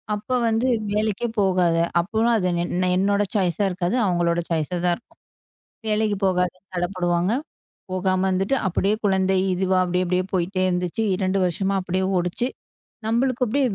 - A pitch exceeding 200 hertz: No, medium, 185 Hz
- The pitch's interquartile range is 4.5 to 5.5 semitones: No, narrow, 2.5 semitones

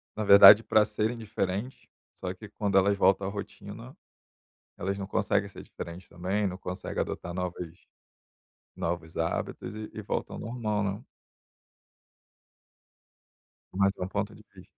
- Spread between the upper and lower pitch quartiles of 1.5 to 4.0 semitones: Yes, narrow, 2.5 semitones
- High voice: No, low, 100 Hz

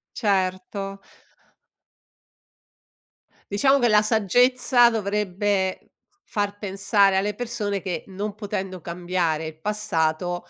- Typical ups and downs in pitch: No, narrow, 2.3 semitones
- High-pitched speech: Yes, high, 200 Hz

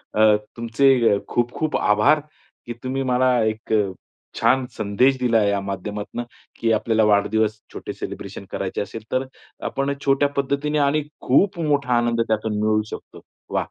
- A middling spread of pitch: Yes, average, 4.0 semitones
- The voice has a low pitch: Yes, low, 115 Hz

